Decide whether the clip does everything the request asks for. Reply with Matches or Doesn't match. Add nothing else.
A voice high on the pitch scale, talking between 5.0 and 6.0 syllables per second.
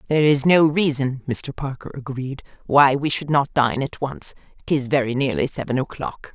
Doesn't match